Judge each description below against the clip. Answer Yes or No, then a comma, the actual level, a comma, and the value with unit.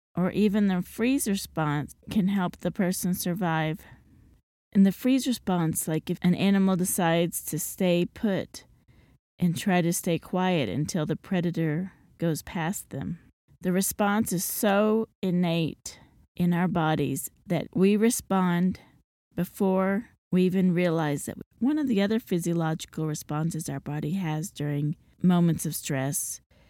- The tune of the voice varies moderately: Yes, average, 3.4 semitones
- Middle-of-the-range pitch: Yes, medium, 180 Hz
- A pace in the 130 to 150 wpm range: Yes, average, 140 wpm